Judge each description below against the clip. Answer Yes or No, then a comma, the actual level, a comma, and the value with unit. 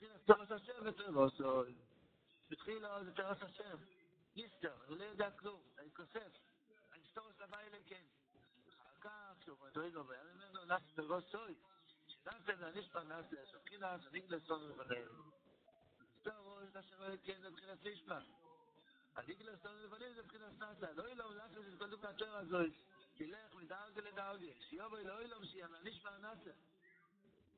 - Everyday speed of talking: No, fast, 160 wpm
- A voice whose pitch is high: Yes, high, 200 Hz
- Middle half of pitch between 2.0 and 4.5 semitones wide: Yes, average, 3.8 semitones